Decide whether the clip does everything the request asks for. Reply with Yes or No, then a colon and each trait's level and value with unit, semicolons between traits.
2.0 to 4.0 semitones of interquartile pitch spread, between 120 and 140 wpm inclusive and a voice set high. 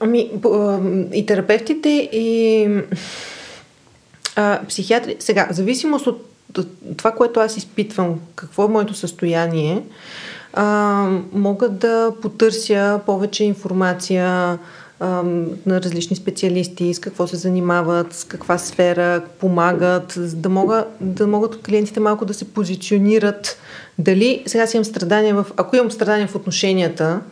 Yes: average, 3.1 semitones; average, 125 wpm; high, 200 Hz